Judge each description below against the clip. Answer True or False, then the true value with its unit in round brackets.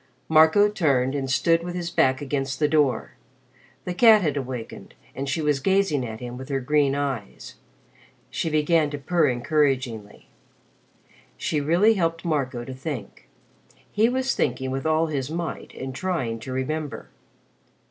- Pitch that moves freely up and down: False (4.0 semitones)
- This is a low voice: False (145 Hz)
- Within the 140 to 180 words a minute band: True (155 wpm)